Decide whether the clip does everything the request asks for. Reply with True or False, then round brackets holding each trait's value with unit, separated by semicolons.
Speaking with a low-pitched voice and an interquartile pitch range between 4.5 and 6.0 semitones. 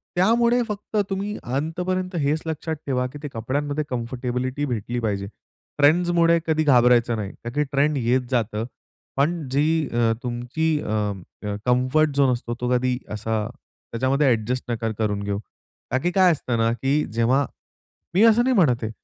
True (130 Hz; 5.1 semitones)